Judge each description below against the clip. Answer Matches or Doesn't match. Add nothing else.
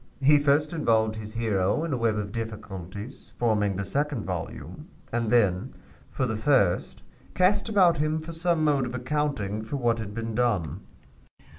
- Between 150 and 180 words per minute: Matches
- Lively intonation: Matches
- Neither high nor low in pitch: Doesn't match